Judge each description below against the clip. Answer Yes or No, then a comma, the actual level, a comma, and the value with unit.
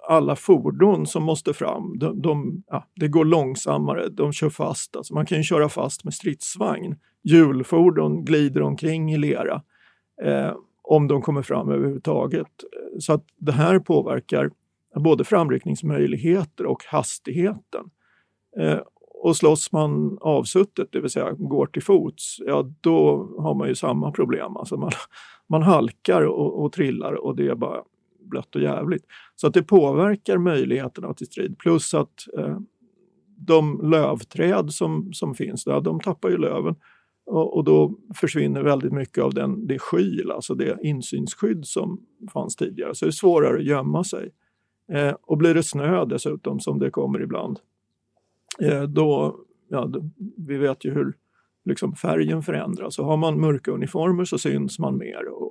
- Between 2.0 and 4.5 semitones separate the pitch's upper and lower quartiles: No, wide, 5.4 semitones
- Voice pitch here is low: No, medium, 155 Hz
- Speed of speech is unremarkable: Yes, average, 160 wpm